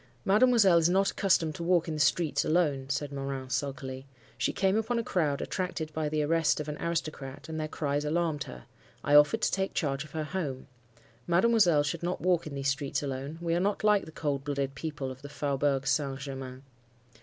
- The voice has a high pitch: No, medium, 150 Hz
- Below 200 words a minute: No, fast, 205 wpm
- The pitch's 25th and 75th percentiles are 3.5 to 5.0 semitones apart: Yes, average, 3.8 semitones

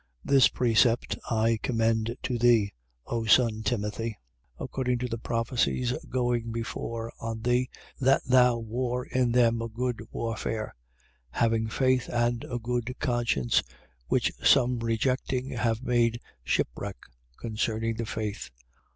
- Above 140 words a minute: No, slow, 135 wpm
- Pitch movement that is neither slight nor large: No, narrow, 1.6 semitones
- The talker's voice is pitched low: Yes, low, 115 Hz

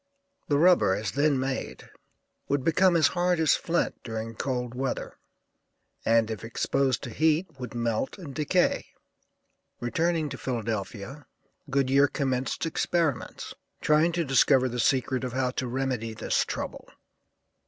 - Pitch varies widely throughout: No, average, 4.2 semitones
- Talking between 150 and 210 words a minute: No, slow, 135 wpm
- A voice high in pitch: No, low, 135 Hz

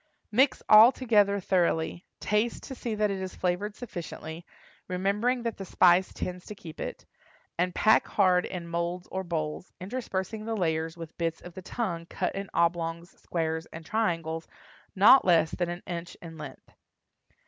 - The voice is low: No, medium, 180 Hz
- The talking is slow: No, average, 165 wpm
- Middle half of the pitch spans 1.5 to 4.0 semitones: Yes, average, 3.7 semitones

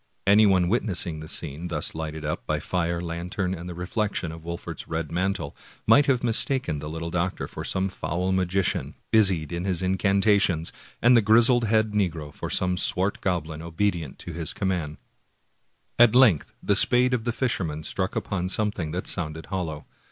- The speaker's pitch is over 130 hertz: No, very low, 90 Hz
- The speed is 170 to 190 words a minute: Yes, average, 175 wpm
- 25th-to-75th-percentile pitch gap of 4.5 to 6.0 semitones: No, average, 3.8 semitones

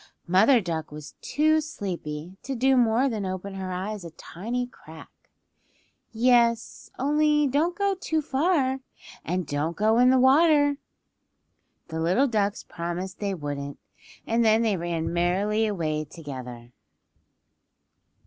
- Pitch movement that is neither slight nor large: No, wide, 7.5 semitones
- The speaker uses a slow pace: Yes, slow, 130 wpm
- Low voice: No, high, 210 Hz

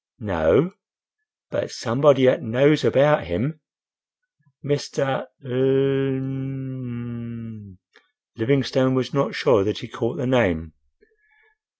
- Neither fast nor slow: No, slow, 90 wpm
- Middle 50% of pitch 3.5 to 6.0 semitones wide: No, narrow, 2.5 semitones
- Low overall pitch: Yes, low, 130 Hz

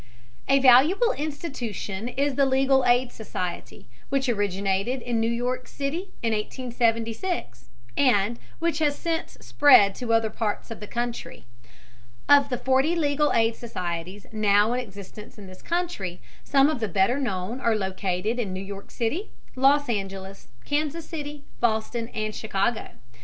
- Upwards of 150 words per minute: No, average, 145 wpm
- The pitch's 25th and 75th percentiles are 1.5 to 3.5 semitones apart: No, average, 5.3 semitones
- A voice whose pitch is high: Yes, high, 235 Hz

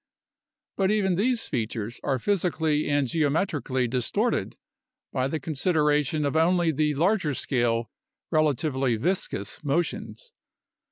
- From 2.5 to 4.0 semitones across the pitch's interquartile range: No, average, 4.7 semitones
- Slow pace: Yes, slow, 115 wpm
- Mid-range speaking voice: Yes, medium, 150 Hz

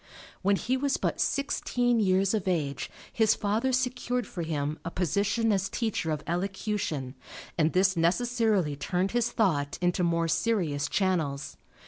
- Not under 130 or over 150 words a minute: Yes, average, 145 wpm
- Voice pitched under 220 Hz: Yes, high, 190 Hz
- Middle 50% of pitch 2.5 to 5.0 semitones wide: No, wide, 5.4 semitones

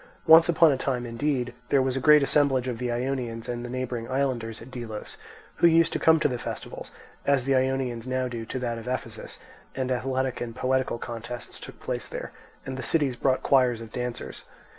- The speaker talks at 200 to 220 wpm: Yes, fast, 205 wpm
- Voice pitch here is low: Yes, low, 130 Hz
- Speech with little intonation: Yes, narrow, 2.0 semitones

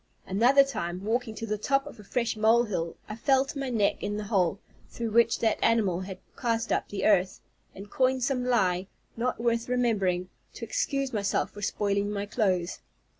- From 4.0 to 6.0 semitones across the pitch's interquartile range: No, average, 3.6 semitones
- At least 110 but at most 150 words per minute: No, average, 185 wpm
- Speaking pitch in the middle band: No, high, 220 Hz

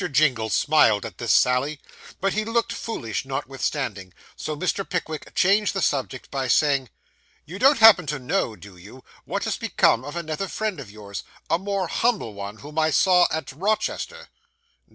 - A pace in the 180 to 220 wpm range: No, average, 170 wpm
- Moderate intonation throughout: No, wide, 7.3 semitones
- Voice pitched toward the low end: No, medium, 150 Hz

